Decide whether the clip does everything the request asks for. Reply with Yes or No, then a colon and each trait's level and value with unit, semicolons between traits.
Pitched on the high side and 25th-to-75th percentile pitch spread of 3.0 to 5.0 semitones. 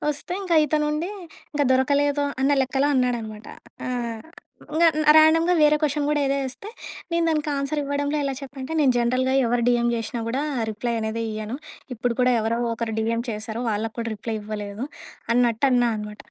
Yes: very high, 255 Hz; average, 4.0 semitones